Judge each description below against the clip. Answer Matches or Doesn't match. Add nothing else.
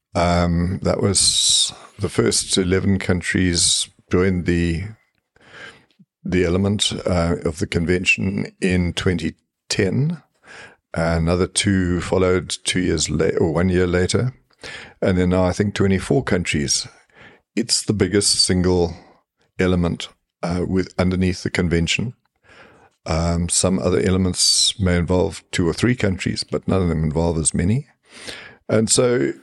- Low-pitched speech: Matches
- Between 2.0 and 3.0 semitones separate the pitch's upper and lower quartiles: Matches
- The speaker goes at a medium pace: Doesn't match